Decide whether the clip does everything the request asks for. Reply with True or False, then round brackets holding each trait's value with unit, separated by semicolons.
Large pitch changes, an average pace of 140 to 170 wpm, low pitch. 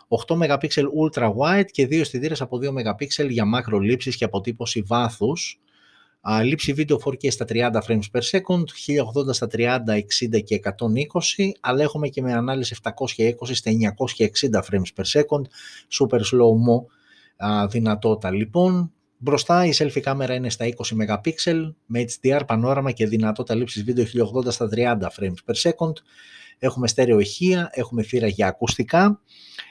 False (4.4 semitones; 145 wpm; 125 Hz)